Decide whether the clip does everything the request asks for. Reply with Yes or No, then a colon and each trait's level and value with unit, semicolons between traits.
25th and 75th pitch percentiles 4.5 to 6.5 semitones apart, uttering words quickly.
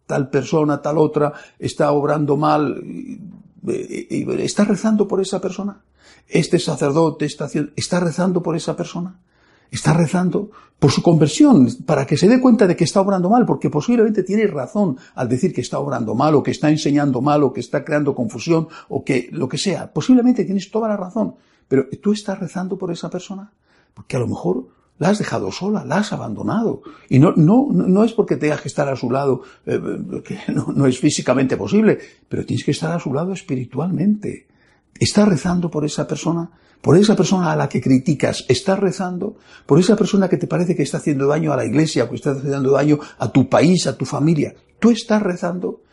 Yes: average, 5.0 semitones; fast, 200 wpm